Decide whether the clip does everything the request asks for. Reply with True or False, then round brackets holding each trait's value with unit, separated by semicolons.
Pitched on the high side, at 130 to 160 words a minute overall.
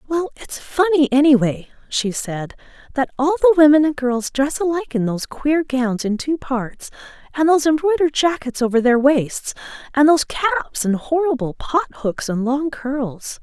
False (280 Hz; 170 wpm)